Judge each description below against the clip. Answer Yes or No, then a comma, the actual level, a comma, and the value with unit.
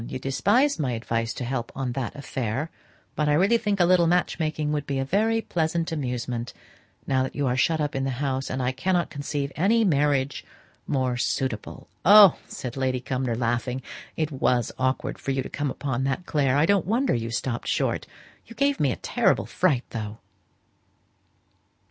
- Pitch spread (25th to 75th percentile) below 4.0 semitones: No, average, 4.6 semitones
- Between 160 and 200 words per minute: Yes, average, 185 wpm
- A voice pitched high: No, low, 135 Hz